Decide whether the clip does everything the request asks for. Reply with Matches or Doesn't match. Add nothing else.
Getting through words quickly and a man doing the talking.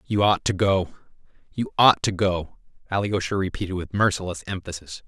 Doesn't match